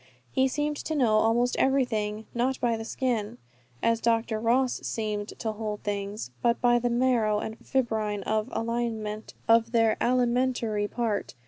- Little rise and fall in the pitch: Yes, narrow, 2.3 semitones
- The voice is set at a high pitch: Yes, high, 230 Hz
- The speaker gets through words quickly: No, average, 140 wpm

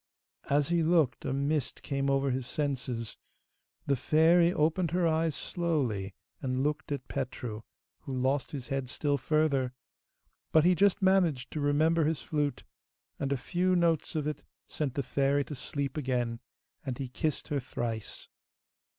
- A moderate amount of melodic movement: Yes, average, 3.4 semitones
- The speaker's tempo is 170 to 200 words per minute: No, average, 160 wpm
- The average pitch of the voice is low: No, medium, 145 Hz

